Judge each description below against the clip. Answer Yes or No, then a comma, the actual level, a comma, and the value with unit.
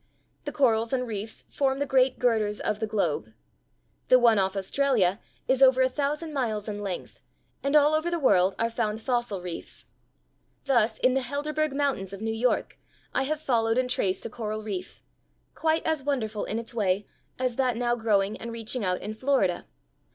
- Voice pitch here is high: Yes, high, 235 Hz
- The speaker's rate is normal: Yes, average, 185 wpm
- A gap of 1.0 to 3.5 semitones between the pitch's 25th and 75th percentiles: No, average, 4.1 semitones